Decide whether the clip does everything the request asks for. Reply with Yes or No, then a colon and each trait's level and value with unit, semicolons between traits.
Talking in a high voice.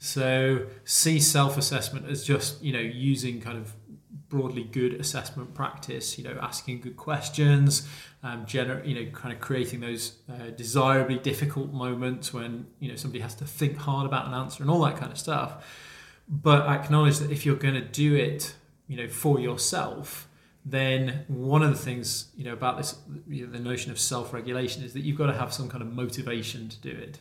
No: low, 135 Hz